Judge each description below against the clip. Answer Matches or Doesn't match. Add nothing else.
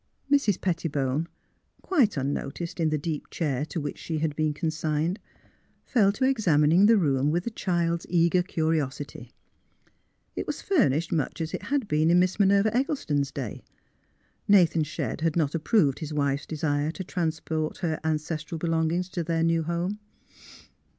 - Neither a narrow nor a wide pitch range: Matches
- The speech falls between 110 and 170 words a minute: Matches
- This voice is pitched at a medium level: Matches